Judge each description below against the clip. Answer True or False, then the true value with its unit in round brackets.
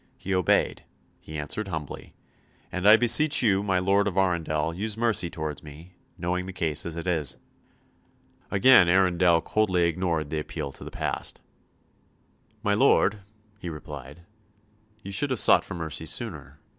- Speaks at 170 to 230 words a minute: False (155 wpm)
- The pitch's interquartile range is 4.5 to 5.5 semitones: False (4.0 semitones)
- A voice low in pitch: True (90 Hz)